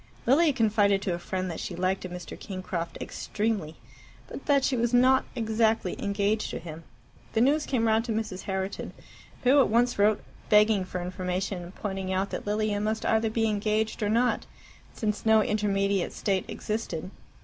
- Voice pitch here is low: No, high, 210 Hz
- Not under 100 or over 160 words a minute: No, average, 175 wpm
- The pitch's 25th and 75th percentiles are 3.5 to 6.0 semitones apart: No, average, 3.0 semitones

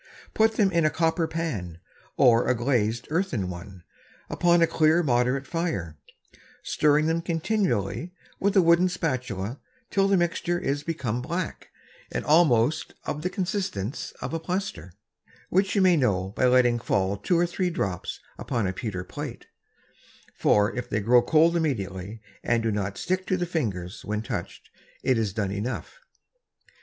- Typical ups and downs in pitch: No, wide, 8.5 semitones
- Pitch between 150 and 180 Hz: No, low, 135 Hz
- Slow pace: No, average, 160 wpm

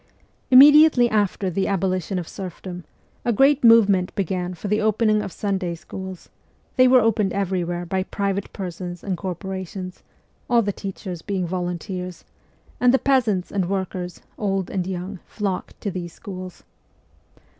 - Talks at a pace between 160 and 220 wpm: No, average, 145 wpm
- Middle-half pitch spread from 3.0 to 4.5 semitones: No, narrow, 2.6 semitones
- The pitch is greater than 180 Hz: Yes, high, 190 Hz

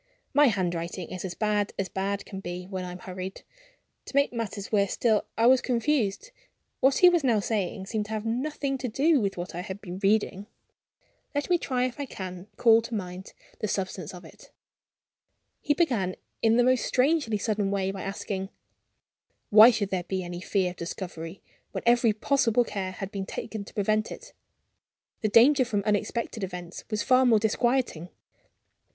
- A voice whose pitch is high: Yes, high, 210 Hz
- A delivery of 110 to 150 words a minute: No, average, 180 wpm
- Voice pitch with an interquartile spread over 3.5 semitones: Yes, average, 4.3 semitones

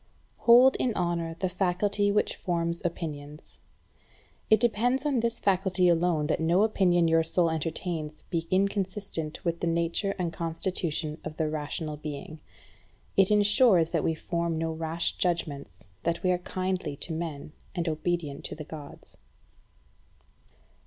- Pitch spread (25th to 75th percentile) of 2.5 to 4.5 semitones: Yes, average, 2.9 semitones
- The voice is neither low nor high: Yes, medium, 170 Hz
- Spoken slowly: No, average, 145 wpm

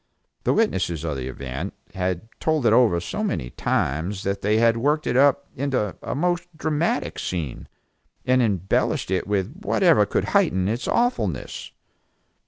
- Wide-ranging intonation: Yes, wide, 7.7 semitones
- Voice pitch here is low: Yes, low, 105 Hz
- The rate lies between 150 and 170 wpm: Yes, average, 155 wpm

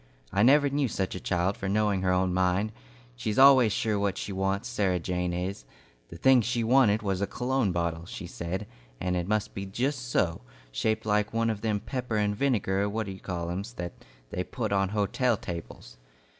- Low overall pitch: Yes, low, 100 Hz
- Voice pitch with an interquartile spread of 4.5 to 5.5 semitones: No, average, 3.5 semitones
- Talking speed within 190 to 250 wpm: Yes, average, 200 wpm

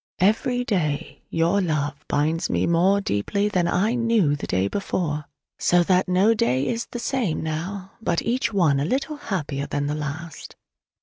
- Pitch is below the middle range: No, medium, 175 Hz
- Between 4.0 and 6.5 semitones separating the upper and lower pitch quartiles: Yes, wide, 5.5 semitones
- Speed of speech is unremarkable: Yes, average, 170 wpm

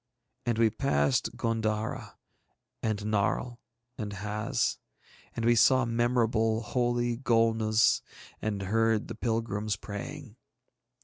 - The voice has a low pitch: Yes, low, 115 Hz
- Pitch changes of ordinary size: No, narrow, 2.0 semitones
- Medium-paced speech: No, slow, 105 wpm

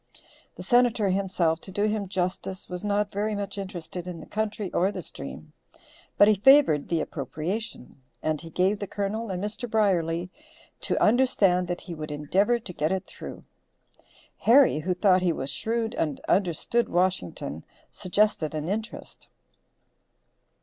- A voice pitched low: No, high, 190 Hz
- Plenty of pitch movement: No, average, 3.9 semitones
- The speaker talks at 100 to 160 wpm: Yes, average, 155 wpm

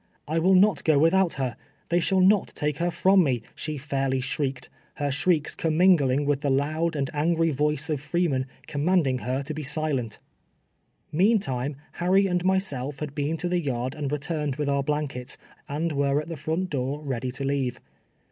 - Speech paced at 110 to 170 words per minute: No, average, 180 wpm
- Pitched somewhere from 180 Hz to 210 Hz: No, medium, 150 Hz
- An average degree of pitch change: Yes, average, 3.7 semitones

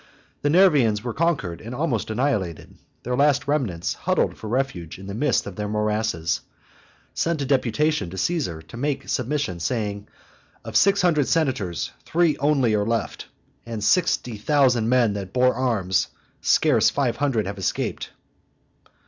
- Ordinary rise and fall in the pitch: No, wide, 5.8 semitones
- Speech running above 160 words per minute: No, average, 155 wpm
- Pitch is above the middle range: No, low, 120 Hz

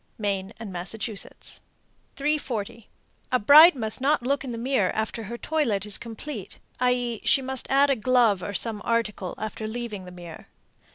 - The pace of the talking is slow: No, average, 165 wpm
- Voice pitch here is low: No, high, 230 Hz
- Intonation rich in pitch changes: No, average, 4.0 semitones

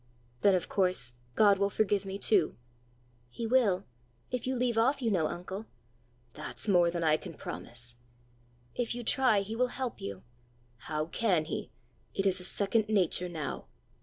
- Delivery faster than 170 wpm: No, average, 165 wpm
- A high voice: Yes, high, 195 Hz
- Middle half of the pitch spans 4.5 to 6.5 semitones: Yes, average, 4.8 semitones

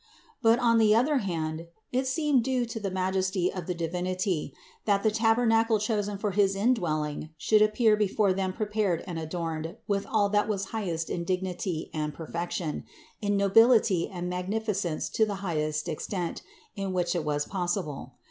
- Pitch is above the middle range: Yes, high, 195 Hz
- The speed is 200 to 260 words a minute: No, average, 170 wpm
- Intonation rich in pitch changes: No, average, 4.0 semitones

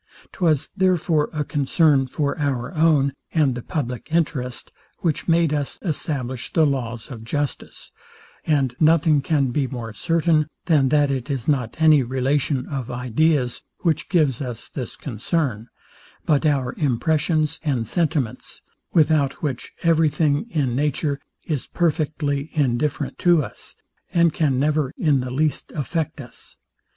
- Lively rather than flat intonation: No, average, 3.3 semitones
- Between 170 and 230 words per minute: No, average, 140 wpm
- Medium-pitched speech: Yes, medium, 145 Hz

